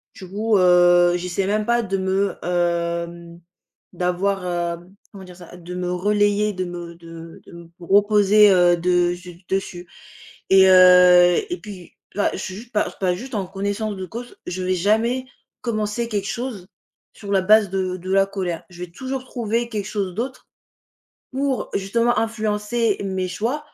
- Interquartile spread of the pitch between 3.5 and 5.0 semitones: No, average, 3.0 semitones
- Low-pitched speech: No, high, 190 Hz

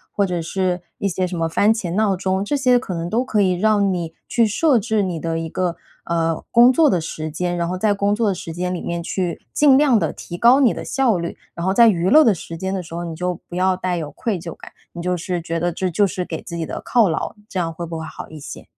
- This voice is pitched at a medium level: Yes, medium, 180 Hz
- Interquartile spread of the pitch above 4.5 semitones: No, average, 3.7 semitones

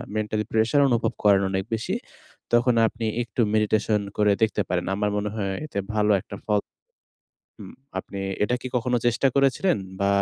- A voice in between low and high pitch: No, low, 110 Hz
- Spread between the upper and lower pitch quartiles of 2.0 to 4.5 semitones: Yes, narrow, 2.4 semitones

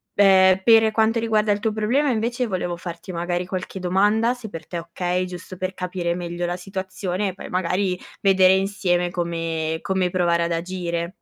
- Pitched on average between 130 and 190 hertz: Yes, medium, 185 Hz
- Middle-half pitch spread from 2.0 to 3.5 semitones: Yes, narrow, 2.6 semitones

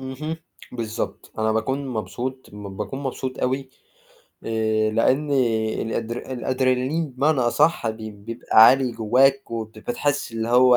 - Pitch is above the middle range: No, low, 120 Hz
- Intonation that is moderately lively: Yes, average, 3.1 semitones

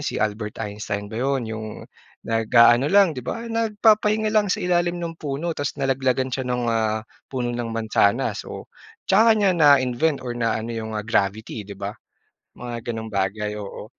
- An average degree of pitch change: No, wide, 6.7 semitones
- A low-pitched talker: Yes, low, 120 Hz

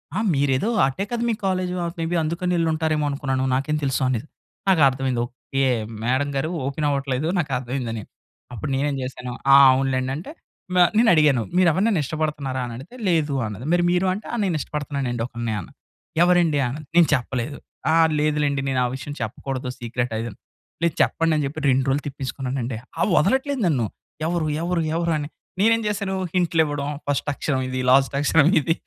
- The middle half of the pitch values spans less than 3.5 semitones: No, average, 4.1 semitones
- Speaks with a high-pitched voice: No, medium, 145 Hz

